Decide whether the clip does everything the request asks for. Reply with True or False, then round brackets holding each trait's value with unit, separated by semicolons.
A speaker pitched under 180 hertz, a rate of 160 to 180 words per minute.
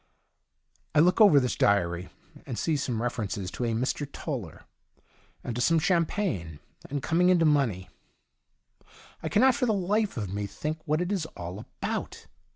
True (140 Hz; 165 wpm)